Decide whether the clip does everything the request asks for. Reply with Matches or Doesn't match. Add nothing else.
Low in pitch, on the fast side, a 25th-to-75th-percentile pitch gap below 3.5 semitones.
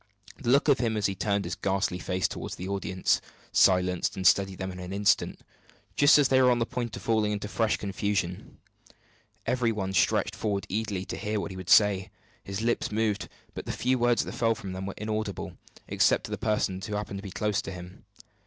Matches